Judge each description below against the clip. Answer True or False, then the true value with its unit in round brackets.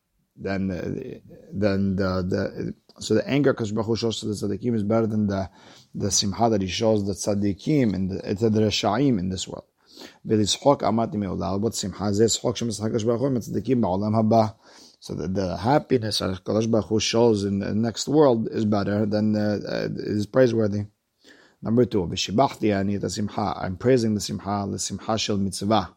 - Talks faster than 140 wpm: False (135 wpm)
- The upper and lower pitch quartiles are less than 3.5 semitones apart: True (2.4 semitones)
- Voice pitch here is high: False (105 Hz)